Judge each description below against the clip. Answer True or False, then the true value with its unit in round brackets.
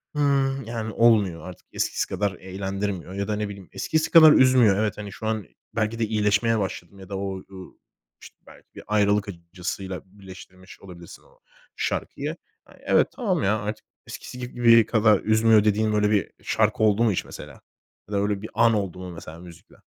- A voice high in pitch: False (105 Hz)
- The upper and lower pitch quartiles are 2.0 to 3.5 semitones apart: True (2.8 semitones)